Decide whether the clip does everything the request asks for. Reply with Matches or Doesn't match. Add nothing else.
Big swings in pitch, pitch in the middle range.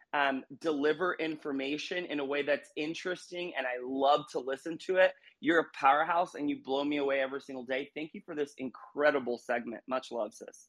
Doesn't match